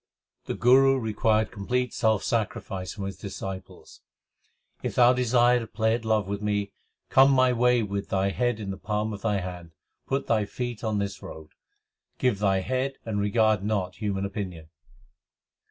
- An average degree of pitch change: Yes, average, 3.6 semitones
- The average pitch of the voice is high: No, low, 105 Hz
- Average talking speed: Yes, average, 170 wpm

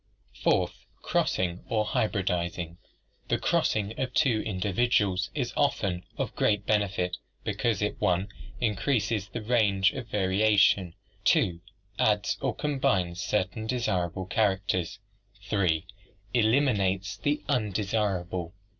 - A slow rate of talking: Yes, slow, 110 wpm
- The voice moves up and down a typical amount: Yes, average, 3.3 semitones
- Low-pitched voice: Yes, low, 100 Hz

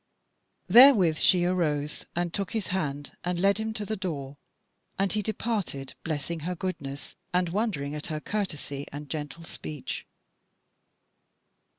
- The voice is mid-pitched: Yes, medium, 175 Hz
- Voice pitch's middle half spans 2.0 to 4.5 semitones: No, average, 5.1 semitones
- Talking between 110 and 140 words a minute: Yes, slow, 135 wpm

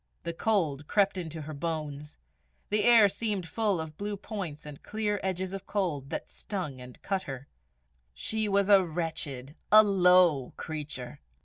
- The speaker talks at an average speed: Yes, average, 155 wpm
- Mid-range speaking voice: Yes, medium, 180 Hz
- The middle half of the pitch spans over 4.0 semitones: Yes, average, 5.2 semitones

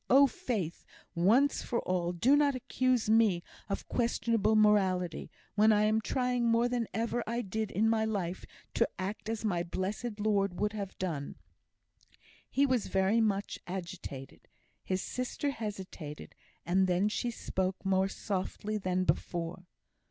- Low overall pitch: No, high, 210 Hz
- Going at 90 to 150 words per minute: Yes, average, 145 wpm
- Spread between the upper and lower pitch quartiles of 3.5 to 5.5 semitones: Yes, average, 3.8 semitones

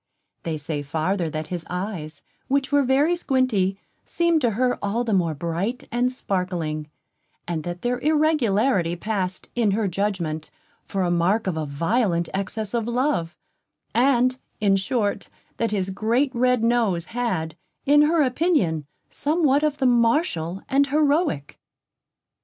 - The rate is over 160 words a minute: No, average, 140 wpm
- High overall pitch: Yes, high, 215 Hz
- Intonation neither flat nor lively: No, wide, 6.8 semitones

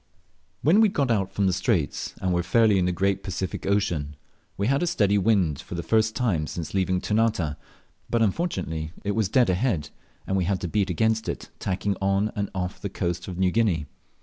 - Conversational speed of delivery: No, fast, 210 wpm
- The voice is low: Yes, very low, 95 Hz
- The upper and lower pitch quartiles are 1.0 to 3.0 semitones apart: No, average, 3.5 semitones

